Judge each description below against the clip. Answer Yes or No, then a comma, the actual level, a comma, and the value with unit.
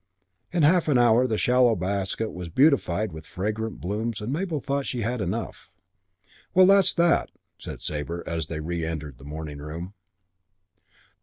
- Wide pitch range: Yes, wide, 7.4 semitones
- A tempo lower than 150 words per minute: No, average, 155 wpm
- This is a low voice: Yes, low, 105 Hz